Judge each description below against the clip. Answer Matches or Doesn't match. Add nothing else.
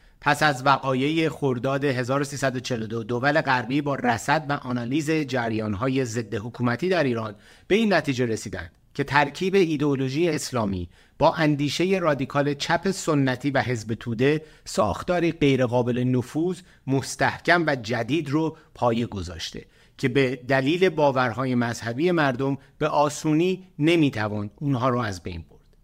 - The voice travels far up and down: Doesn't match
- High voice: Doesn't match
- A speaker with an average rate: Matches